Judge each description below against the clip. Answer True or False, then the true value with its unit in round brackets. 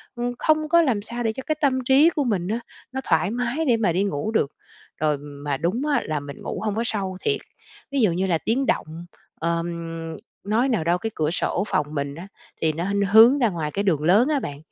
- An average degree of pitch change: False (7.0 semitones)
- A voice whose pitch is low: False (205 Hz)